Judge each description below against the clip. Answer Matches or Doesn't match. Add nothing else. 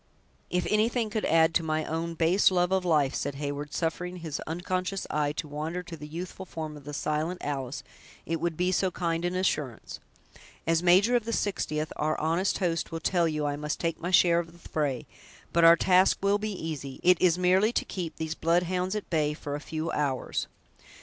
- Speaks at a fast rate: Matches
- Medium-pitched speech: Matches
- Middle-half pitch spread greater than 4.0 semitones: Doesn't match